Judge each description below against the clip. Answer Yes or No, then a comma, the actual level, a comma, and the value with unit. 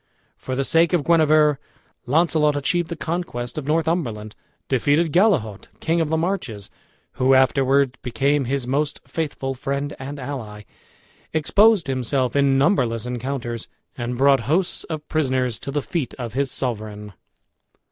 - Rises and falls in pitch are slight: No, average, 4.0 semitones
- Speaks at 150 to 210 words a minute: No, average, 140 wpm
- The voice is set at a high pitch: No, medium, 140 Hz